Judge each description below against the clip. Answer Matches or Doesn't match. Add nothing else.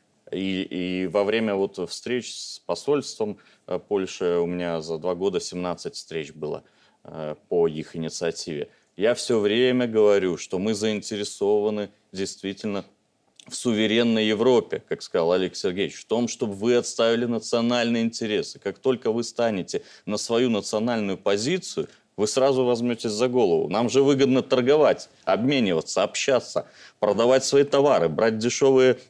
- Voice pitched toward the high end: Doesn't match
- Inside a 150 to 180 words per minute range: Doesn't match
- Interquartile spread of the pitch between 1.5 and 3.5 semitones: Doesn't match